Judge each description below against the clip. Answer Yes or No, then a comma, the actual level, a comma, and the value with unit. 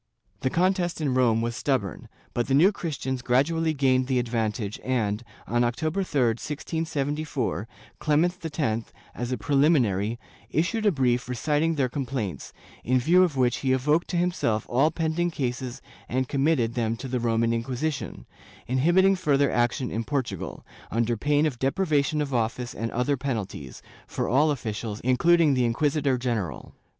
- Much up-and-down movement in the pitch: No, average, 4.3 semitones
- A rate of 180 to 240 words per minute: No, average, 160 wpm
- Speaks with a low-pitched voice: Yes, low, 130 Hz